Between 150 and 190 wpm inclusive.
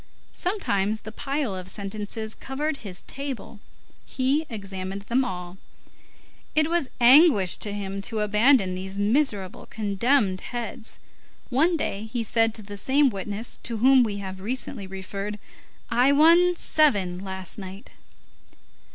No: slow, 135 wpm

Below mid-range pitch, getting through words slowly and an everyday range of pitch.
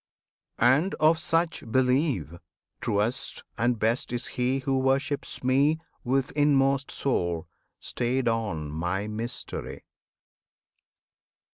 Yes: low, 130 Hz; slow, 100 wpm; average, 3.8 semitones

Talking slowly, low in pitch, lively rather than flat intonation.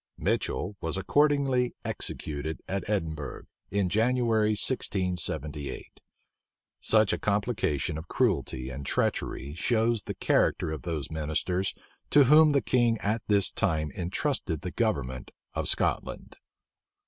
Yes: slow, 120 wpm; very low, 95 Hz; wide, 6.6 semitones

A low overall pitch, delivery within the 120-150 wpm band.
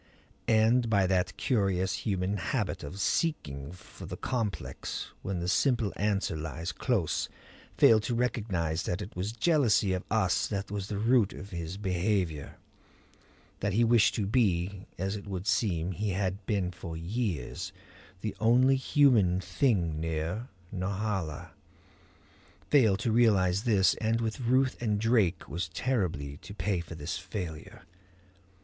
Yes: low, 100 Hz; average, 145 wpm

